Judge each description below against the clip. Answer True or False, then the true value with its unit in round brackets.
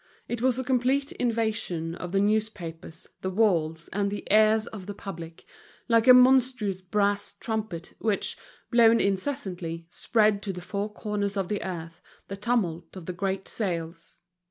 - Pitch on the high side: True (200 Hz)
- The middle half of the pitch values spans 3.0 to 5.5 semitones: True (4.1 semitones)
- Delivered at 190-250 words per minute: False (155 wpm)